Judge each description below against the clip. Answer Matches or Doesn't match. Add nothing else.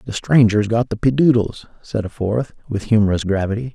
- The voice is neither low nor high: Doesn't match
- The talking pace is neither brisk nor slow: Matches